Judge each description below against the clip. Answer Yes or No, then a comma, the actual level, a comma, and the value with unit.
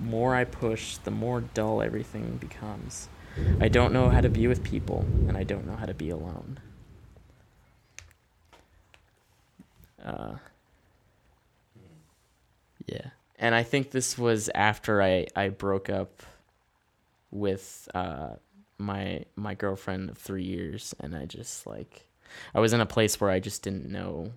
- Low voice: Yes, low, 100 Hz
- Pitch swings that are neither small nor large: Yes, average, 3.4 semitones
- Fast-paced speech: No, average, 145 wpm